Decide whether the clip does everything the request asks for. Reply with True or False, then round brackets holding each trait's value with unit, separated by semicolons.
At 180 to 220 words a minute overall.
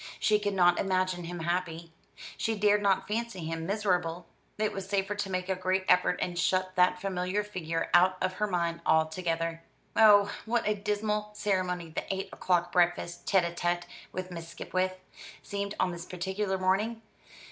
False (170 wpm)